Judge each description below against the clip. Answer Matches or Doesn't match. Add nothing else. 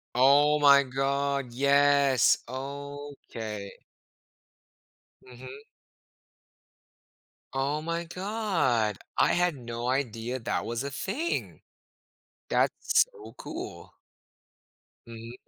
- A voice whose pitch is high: Doesn't match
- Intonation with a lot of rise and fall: Doesn't match